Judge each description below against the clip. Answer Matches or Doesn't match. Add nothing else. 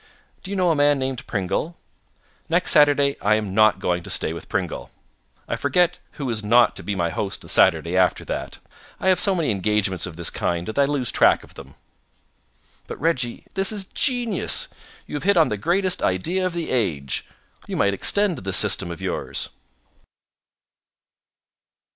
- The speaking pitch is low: Matches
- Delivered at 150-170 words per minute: Doesn't match